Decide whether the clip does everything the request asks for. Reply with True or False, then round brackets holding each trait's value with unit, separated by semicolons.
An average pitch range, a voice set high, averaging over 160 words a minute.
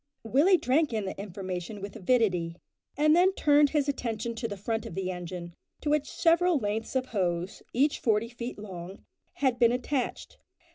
False (6.7 semitones; 230 Hz; 175 wpm)